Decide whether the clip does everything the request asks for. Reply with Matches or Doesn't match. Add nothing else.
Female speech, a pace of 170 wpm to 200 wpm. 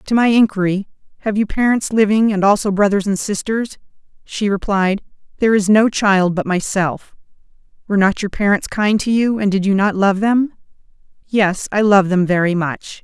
Matches